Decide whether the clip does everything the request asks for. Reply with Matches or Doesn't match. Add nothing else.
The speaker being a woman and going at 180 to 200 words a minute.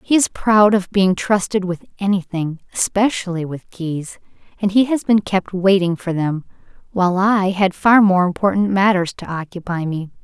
Doesn't match